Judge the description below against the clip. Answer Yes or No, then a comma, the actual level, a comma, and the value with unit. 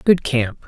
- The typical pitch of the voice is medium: Yes, medium, 175 Hz